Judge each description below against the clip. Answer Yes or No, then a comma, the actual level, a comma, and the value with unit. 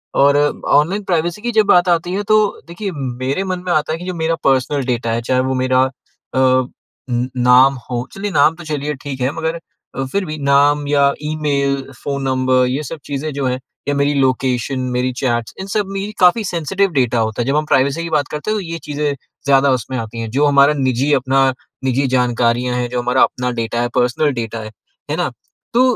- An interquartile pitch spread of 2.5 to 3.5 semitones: No, average, 4.2 semitones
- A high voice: No, medium, 140 Hz